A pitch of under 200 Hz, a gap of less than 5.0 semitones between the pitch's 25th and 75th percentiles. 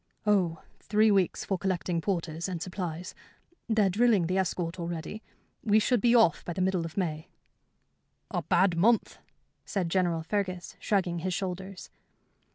Yes: medium, 185 Hz; average, 2.8 semitones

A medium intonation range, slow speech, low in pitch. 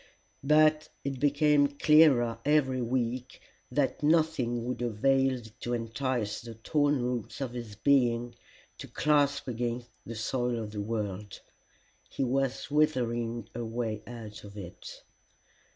Yes: average, 3.5 semitones; slow, 125 wpm; low, 125 Hz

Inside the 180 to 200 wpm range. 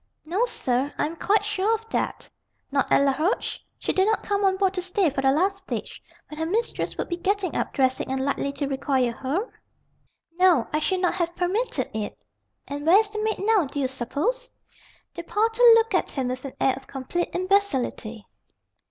Yes: average, 195 wpm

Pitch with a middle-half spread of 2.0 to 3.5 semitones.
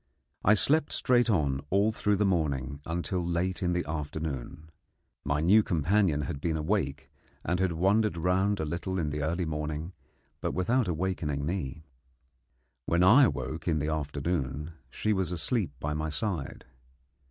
No: average, 4.1 semitones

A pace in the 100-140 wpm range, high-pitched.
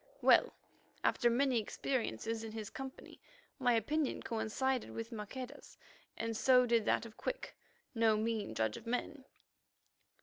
Yes: slow, 135 wpm; high, 230 Hz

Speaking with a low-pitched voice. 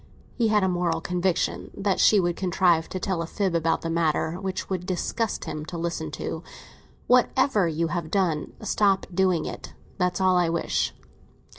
No: medium, 180 Hz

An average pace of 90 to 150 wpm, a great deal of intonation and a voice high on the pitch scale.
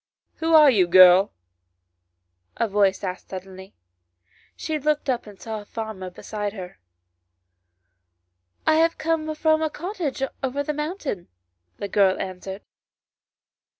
Yes: average, 140 wpm; wide, 8.4 semitones; high, 210 Hz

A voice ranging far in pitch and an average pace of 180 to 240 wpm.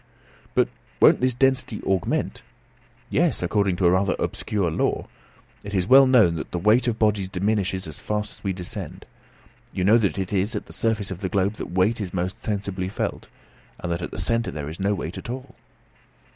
No: average, 3.2 semitones; average, 200 wpm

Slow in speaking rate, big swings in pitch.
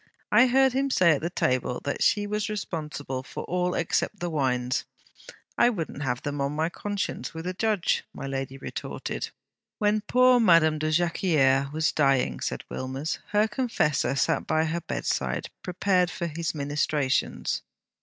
No: average, 155 wpm; wide, 6.6 semitones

